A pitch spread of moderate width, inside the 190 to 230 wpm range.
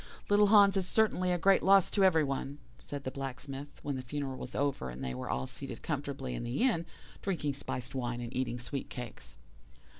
No: wide, 6.8 semitones; fast, 205 wpm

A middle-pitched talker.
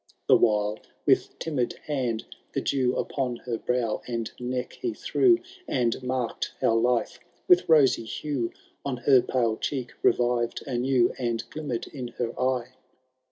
No: low, 125 Hz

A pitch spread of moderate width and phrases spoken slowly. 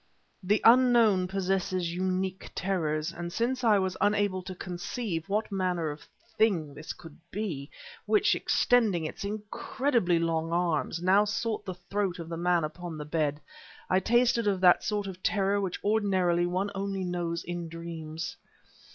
No: average, 3.4 semitones; average, 155 wpm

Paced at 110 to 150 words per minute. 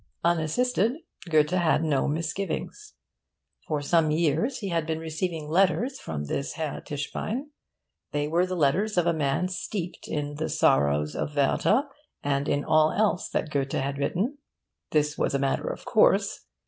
No: average, 160 wpm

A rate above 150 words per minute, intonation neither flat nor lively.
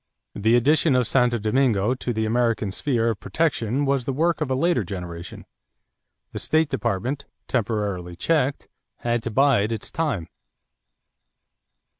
No: average, 140 wpm; average, 4.4 semitones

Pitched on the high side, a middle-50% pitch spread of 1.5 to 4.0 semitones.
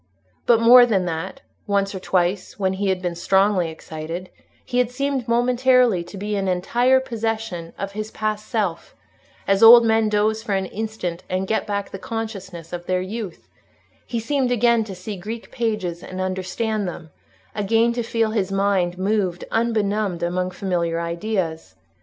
Yes: high, 200 Hz; average, 3.6 semitones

